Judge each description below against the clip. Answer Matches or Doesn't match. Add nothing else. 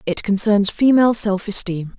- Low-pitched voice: Doesn't match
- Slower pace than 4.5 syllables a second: Doesn't match